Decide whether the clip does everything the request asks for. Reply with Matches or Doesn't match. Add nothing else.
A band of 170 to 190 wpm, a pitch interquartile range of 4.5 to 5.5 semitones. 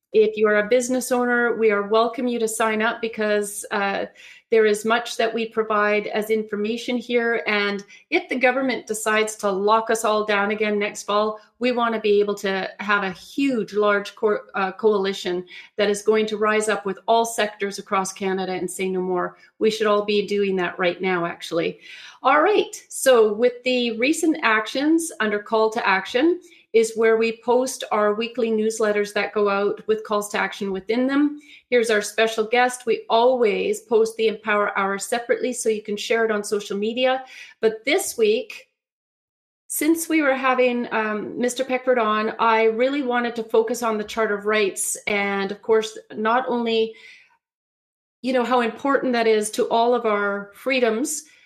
Doesn't match